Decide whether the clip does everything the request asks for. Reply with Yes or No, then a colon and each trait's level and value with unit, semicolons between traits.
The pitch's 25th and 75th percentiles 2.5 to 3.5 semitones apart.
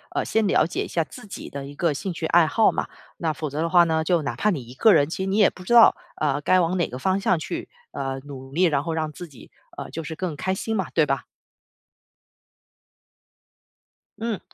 No: average, 4.5 semitones